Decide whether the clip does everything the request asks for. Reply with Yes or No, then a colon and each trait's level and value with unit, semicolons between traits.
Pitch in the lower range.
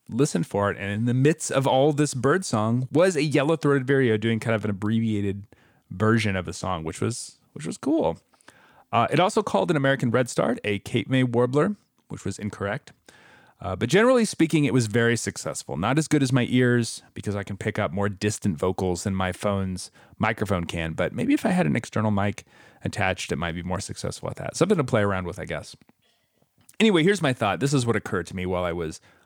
Yes: low, 115 Hz